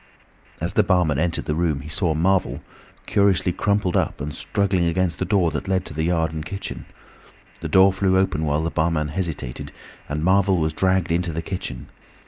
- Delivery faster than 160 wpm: Yes, average, 190 wpm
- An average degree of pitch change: Yes, average, 3.3 semitones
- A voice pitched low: Yes, very low, 85 Hz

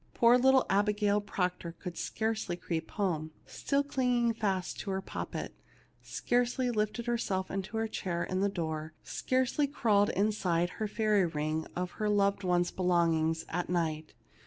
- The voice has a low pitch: No, high, 195 Hz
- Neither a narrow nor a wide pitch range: Yes, average, 4.1 semitones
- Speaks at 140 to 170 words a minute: Yes, average, 155 wpm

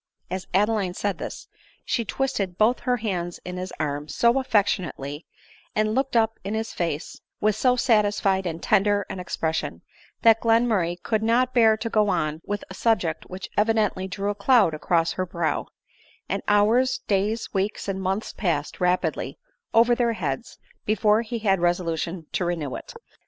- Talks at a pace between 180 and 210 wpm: No, average, 170 wpm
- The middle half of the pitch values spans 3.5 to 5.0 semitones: Yes, average, 4.0 semitones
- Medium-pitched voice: No, high, 205 Hz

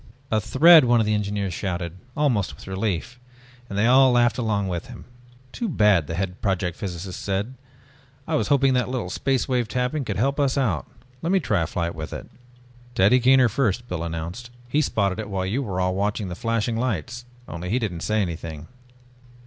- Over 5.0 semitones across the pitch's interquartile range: Yes, wide, 5.4 semitones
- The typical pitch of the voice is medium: No, low, 105 Hz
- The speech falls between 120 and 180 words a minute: No, average, 200 wpm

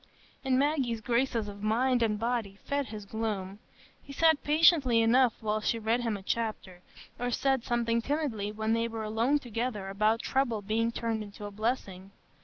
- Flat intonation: No, average, 3.0 semitones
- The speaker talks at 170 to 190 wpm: Yes, average, 175 wpm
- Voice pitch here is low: No, high, 230 Hz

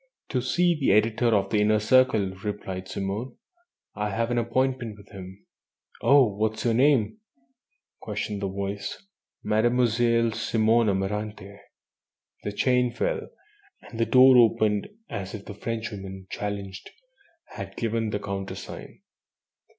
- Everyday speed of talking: No, slow, 130 wpm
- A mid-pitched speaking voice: No, low, 110 Hz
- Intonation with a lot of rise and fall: No, average, 2.9 semitones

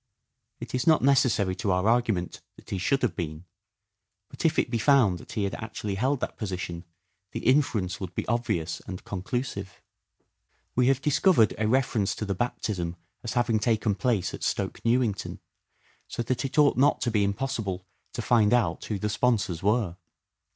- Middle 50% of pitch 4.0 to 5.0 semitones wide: Yes, average, 4.6 semitones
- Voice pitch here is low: Yes, low, 110 Hz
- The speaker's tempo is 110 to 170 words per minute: No, average, 180 wpm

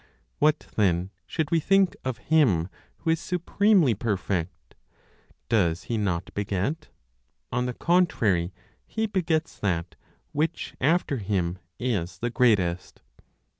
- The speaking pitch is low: Yes, low, 115 Hz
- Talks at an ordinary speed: No, slow, 120 wpm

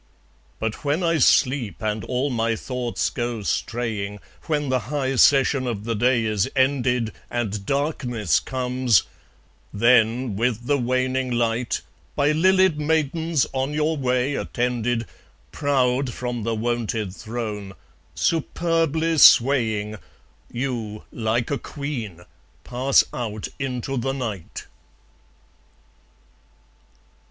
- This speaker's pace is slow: Yes, slow, 110 wpm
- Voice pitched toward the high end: No, low, 125 Hz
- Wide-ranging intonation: No, average, 3.4 semitones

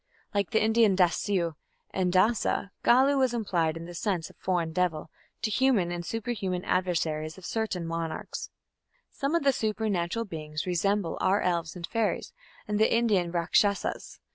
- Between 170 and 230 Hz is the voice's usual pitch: Yes, medium, 185 Hz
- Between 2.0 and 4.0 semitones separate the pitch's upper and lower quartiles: No, average, 4.4 semitones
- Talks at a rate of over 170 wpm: No, average, 155 wpm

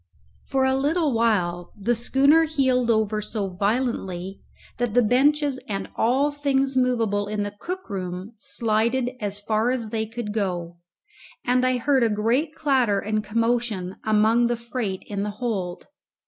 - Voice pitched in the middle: No, high, 230 Hz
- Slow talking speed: No, average, 155 wpm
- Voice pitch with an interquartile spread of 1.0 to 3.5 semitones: No, average, 3.9 semitones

